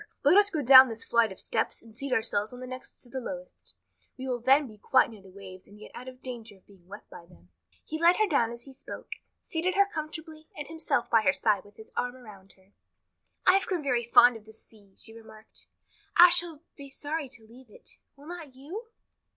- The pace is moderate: No, fast, 230 wpm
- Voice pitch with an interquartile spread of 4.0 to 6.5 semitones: Yes, wide, 5.5 semitones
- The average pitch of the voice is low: No, very high, 250 Hz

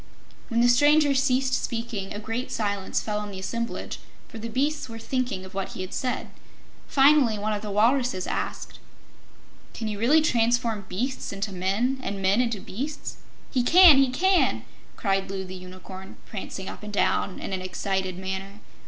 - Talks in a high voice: Yes, high, 220 Hz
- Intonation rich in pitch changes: No, average, 4.7 semitones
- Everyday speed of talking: Yes, average, 175 wpm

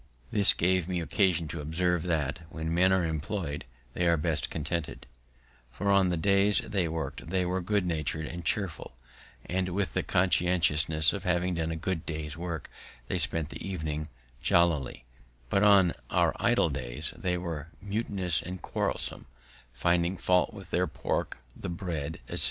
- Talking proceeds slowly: No, average, 165 wpm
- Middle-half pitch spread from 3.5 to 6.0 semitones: No, average, 2.7 semitones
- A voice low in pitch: Yes, very low, 85 Hz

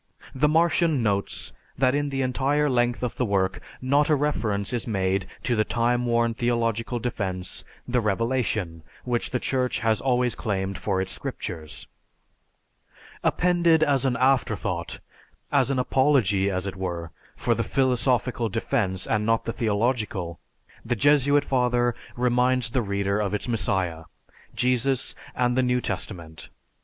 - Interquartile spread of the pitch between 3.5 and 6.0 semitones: Yes, average, 4.4 semitones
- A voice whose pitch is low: Yes, low, 120 Hz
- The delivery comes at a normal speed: Yes, average, 145 wpm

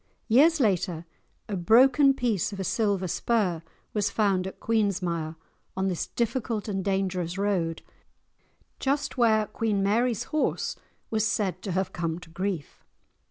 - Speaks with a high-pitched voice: Yes, high, 200 Hz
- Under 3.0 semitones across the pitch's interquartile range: No, average, 3.8 semitones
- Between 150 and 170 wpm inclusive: No, average, 140 wpm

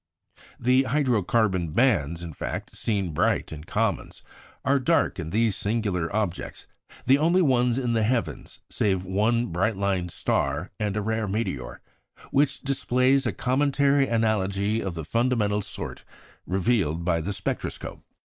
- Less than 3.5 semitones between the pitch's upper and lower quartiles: No, average, 5.3 semitones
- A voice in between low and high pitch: No, low, 105 Hz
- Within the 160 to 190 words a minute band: No, average, 145 wpm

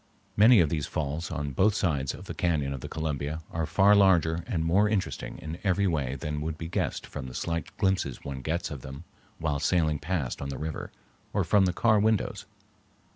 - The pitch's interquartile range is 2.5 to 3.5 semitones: No, average, 4.5 semitones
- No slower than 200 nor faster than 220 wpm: Yes, fast, 205 wpm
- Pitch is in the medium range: No, very low, 80 Hz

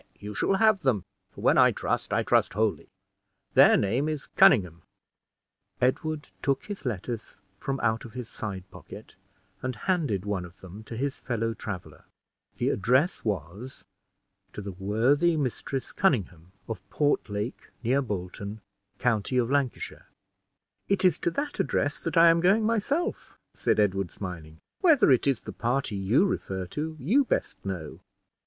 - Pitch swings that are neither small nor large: No, wide, 7.0 semitones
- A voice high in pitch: No, low, 120 Hz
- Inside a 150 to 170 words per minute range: Yes, average, 155 wpm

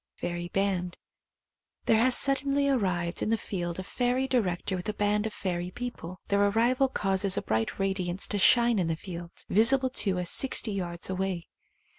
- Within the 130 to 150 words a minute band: No, average, 175 wpm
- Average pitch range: Yes, average, 5.0 semitones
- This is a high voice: Yes, high, 195 Hz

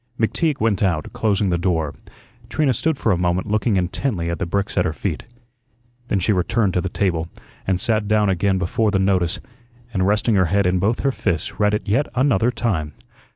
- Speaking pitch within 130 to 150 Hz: No, low, 100 Hz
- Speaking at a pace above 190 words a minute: Yes, average, 200 wpm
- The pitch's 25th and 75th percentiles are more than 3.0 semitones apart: Yes, average, 3.4 semitones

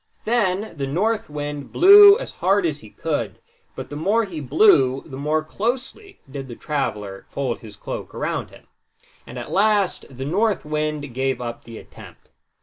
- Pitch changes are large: Yes, wide, 7.5 semitones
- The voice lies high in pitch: No, medium, 150 Hz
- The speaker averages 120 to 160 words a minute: No, average, 170 wpm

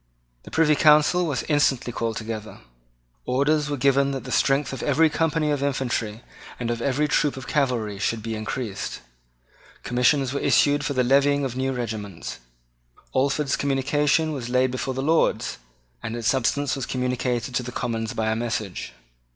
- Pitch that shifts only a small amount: No, average, 3.3 semitones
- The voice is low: Yes, low, 130 Hz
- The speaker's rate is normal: Yes, average, 165 wpm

